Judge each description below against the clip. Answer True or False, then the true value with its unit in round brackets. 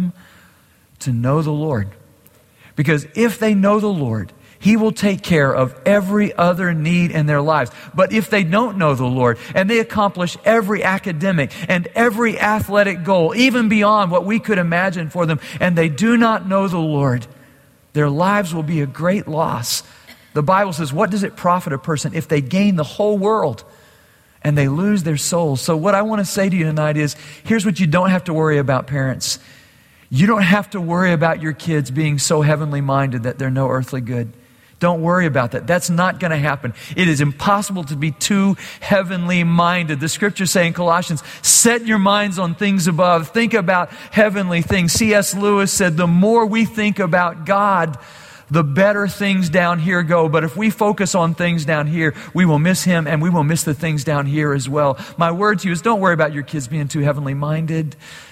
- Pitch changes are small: False (4.9 semitones)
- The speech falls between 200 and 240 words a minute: True (205 wpm)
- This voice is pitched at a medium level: True (170 Hz)